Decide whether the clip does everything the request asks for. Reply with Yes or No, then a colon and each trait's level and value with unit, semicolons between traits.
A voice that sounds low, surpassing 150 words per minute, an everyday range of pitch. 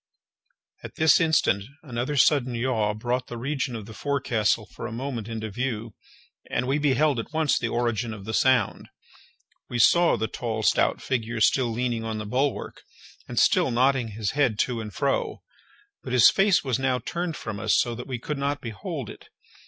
Yes: low, 120 Hz; average, 185 wpm; average, 3.6 semitones